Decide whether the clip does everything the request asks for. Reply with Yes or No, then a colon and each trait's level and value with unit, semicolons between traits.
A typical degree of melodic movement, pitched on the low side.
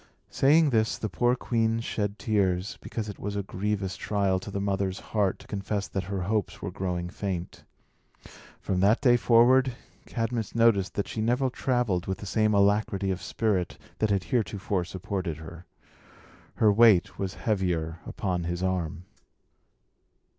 Yes: average, 3.1 semitones; low, 100 Hz